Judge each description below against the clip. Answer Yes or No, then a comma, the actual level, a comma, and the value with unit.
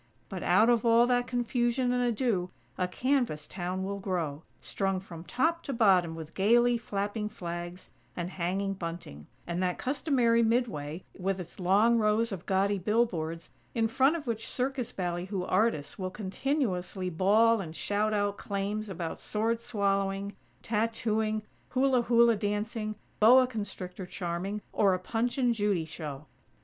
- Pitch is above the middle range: Yes, high, 205 Hz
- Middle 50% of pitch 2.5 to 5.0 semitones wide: Yes, average, 4.3 semitones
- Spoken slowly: No, average, 150 wpm